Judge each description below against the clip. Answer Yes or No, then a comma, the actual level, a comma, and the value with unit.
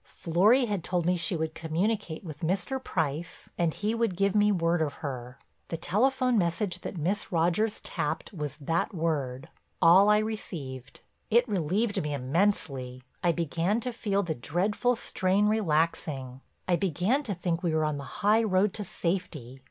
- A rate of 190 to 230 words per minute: No, average, 165 wpm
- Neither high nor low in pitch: Yes, medium, 175 Hz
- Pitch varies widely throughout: No, average, 4.9 semitones